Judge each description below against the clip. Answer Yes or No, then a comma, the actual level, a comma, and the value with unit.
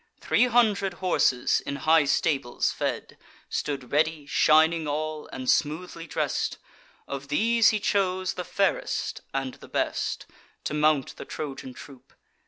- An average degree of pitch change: Yes, average, 4.6 semitones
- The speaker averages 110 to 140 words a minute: Yes, slow, 135 wpm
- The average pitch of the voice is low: No, medium, 155 Hz